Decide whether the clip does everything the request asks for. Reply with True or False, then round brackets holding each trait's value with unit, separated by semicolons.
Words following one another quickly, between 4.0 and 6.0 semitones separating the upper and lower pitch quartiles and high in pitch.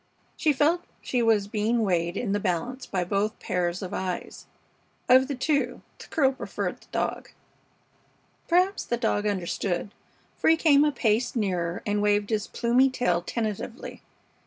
False (160 wpm; 4.9 semitones; 220 Hz)